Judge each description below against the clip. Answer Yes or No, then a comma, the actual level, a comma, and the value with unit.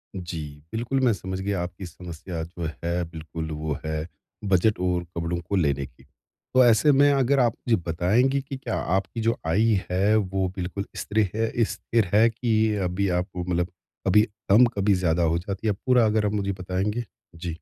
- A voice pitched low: Yes, very low, 95 Hz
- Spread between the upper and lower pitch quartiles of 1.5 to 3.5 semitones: No, average, 4.2 semitones